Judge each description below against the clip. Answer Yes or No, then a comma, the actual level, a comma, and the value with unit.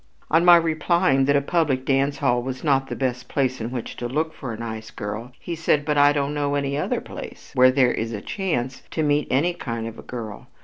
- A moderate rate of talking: No, fast, 235 wpm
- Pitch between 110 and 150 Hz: Yes, low, 135 Hz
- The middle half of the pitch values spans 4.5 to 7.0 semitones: No, average, 3.5 semitones